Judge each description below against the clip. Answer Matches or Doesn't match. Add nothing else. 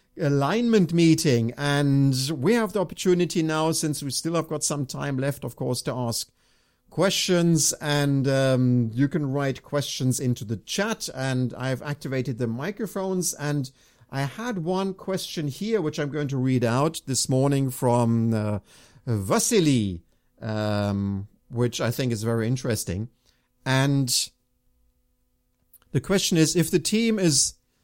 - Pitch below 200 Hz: Matches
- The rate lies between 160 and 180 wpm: Doesn't match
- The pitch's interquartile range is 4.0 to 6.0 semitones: Matches